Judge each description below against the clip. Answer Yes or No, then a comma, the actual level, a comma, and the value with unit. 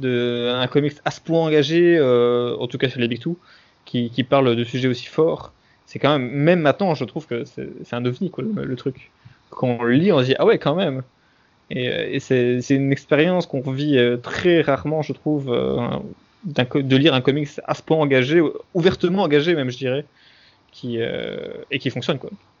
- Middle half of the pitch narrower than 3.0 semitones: No, average, 4.1 semitones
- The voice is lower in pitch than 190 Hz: Yes, low, 135 Hz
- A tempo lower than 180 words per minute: No, fast, 220 wpm